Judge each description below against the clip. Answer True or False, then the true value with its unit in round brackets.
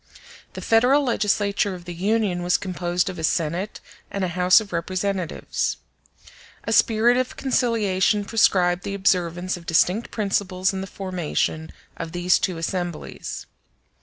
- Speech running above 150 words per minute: False (140 wpm)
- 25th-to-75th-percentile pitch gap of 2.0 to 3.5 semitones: True (2.7 semitones)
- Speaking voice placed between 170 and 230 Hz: True (185 Hz)